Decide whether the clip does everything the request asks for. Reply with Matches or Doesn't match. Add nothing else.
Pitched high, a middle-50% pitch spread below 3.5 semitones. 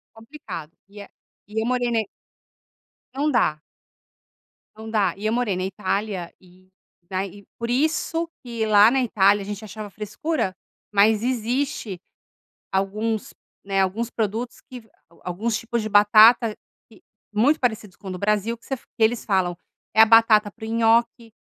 Matches